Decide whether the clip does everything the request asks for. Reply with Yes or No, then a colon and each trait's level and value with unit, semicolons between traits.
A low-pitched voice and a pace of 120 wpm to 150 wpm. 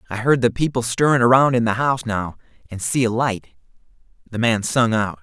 No: low, 120 Hz; fast, 205 wpm